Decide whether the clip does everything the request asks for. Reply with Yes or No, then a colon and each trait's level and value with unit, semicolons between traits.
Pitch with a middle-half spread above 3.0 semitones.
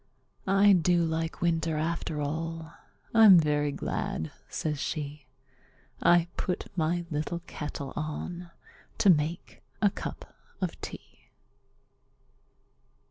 No: narrow, 2.6 semitones